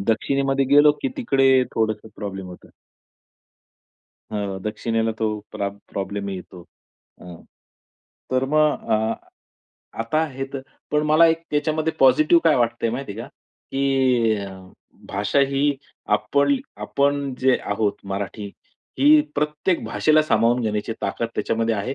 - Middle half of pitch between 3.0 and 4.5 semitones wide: No, average, 5.0 semitones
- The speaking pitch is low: Yes, low, 125 Hz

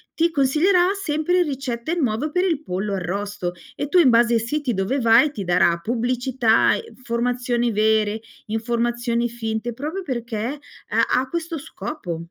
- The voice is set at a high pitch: Yes, high, 240 Hz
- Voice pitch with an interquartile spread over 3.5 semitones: Yes, average, 4.9 semitones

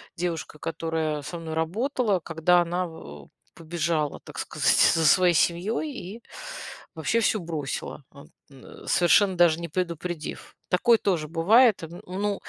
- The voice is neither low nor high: Yes, medium, 170 Hz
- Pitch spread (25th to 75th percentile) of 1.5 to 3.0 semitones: Yes, narrow, 2.6 semitones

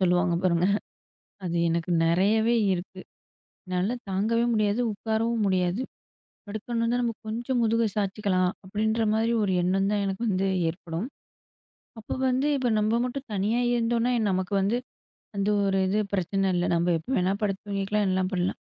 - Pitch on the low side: No, high, 200 Hz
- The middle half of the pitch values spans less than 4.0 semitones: Yes, average, 3.5 semitones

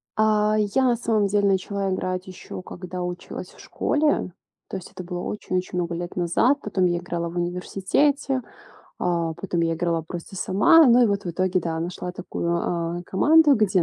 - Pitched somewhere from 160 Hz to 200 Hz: Yes, medium, 185 Hz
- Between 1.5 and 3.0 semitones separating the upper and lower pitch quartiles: No, average, 3.4 semitones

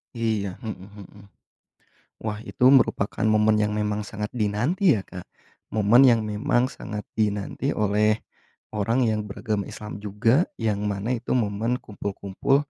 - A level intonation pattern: Yes, narrow, 1.9 semitones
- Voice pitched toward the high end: No, low, 105 Hz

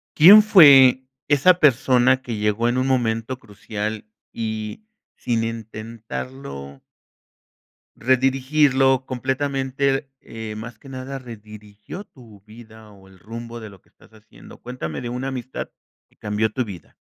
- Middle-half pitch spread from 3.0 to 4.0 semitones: Yes, average, 3.5 semitones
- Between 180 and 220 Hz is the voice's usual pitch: No, low, 120 Hz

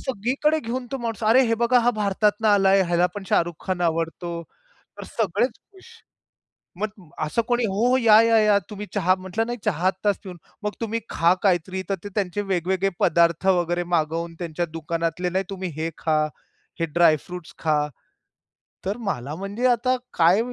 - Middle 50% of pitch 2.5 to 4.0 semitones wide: No, average, 4.7 semitones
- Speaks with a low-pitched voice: No, high, 190 Hz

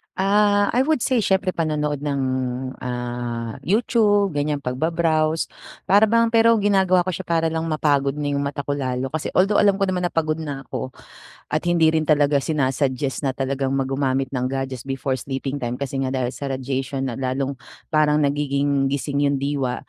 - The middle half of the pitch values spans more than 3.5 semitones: Yes, average, 4.0 semitones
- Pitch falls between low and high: Yes, medium, 145 Hz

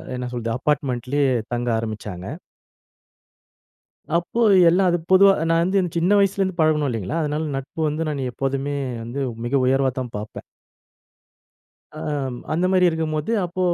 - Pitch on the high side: No, medium, 150 Hz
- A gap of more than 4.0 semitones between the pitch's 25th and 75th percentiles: Yes, average, 5.2 semitones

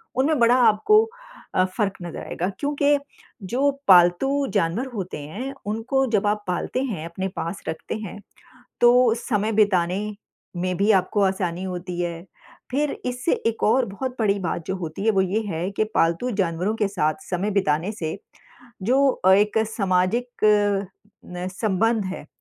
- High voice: Yes, high, 200 Hz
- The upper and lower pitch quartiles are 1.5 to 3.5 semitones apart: No, average, 4.4 semitones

